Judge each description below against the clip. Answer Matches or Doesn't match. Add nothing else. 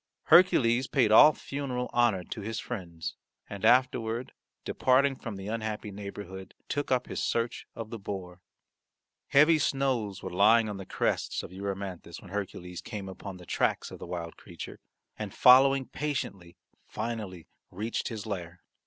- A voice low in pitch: Matches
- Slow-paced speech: Doesn't match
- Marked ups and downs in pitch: Doesn't match